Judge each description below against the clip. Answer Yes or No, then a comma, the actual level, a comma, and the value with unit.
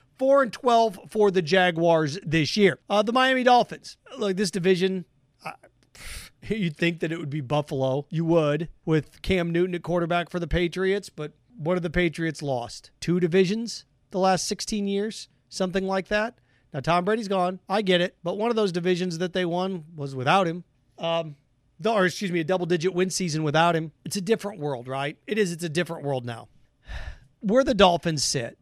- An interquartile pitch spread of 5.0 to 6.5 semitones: No, average, 3.7 semitones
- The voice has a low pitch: No, medium, 180 Hz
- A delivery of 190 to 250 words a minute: Yes, average, 195 wpm